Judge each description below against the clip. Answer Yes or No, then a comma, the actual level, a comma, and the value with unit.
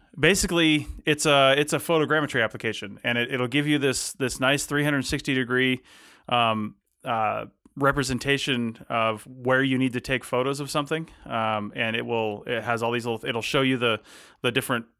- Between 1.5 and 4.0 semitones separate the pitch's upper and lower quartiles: Yes, average, 3.5 semitones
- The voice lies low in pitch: Yes, low, 130 Hz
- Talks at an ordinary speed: Yes, average, 190 wpm